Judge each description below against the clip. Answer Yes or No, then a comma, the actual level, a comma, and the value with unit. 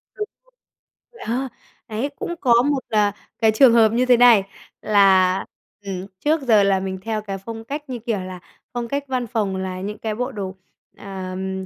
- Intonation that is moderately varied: Yes, average, 4.2 semitones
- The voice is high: Yes, high, 215 Hz